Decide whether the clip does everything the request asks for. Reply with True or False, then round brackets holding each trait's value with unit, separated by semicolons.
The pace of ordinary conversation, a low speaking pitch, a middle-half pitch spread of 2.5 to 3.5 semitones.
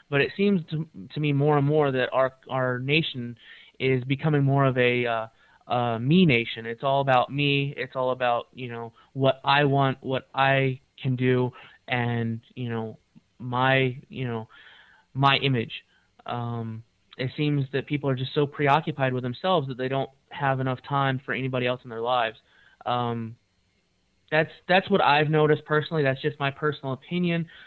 True (175 wpm; 130 Hz; 2.8 semitones)